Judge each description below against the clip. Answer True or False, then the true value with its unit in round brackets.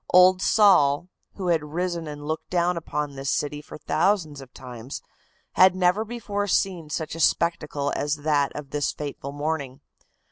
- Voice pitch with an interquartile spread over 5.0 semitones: False (3.8 semitones)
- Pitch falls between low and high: True (155 Hz)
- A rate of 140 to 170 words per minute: True (165 wpm)